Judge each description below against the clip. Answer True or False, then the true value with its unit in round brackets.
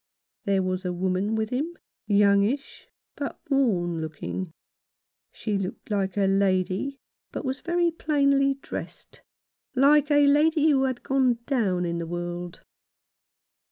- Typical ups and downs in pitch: False (7.1 semitones)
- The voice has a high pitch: True (215 Hz)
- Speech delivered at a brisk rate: False (135 wpm)